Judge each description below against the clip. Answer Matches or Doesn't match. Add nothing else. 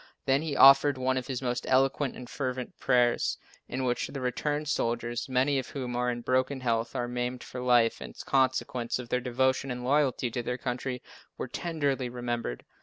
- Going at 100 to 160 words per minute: Doesn't match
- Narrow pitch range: Matches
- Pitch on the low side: Matches